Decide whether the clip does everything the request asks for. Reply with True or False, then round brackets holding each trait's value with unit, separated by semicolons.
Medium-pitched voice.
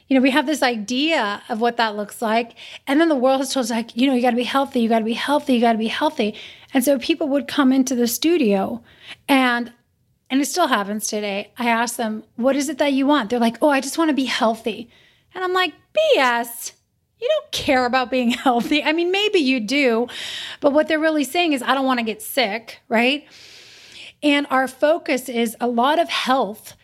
False (260 Hz)